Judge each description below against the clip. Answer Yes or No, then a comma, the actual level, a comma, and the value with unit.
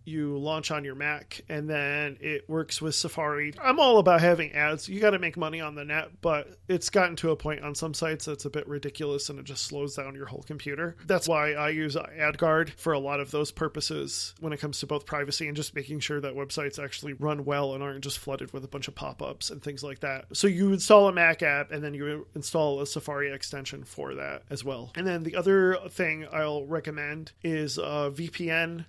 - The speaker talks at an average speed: No, fast, 235 wpm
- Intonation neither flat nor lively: No, narrow, 2.1 semitones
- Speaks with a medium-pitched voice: Yes, medium, 150 Hz